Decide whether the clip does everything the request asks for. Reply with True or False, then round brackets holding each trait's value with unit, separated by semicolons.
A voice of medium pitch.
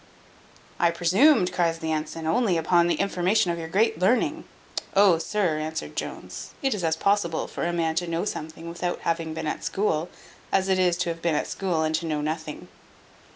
True (170 Hz)